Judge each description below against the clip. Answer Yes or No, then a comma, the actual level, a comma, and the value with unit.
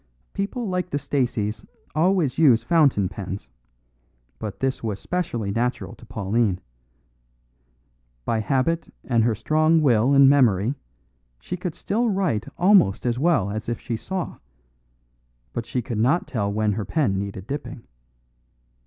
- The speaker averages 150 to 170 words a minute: No, average, 140 wpm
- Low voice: Yes, low, 125 Hz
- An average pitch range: No, wide, 7.0 semitones